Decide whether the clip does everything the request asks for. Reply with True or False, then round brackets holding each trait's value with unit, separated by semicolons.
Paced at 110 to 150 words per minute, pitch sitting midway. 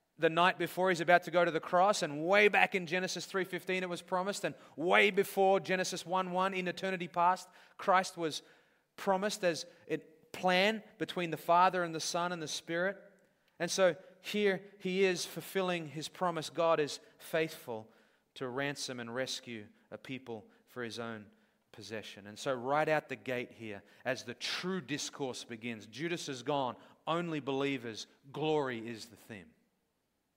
False (165 wpm; 170 Hz)